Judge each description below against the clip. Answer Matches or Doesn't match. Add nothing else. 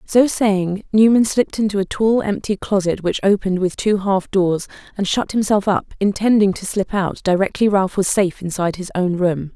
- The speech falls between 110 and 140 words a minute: Doesn't match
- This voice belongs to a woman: Matches